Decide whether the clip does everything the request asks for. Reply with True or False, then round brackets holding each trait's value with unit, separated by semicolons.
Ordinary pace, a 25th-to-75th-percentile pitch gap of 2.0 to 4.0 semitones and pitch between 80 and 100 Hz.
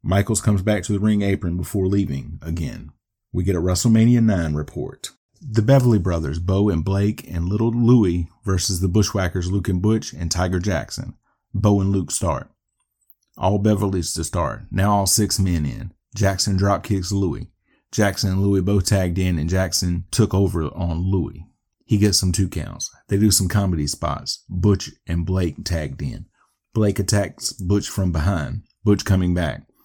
True (175 wpm; 2.7 semitones; 95 Hz)